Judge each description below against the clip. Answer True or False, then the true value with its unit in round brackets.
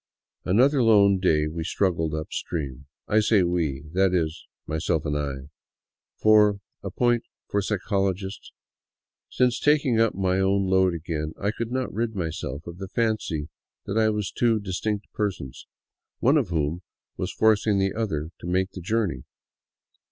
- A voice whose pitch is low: True (95 Hz)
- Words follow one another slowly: False (170 wpm)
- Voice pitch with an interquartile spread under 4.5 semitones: False (4.9 semitones)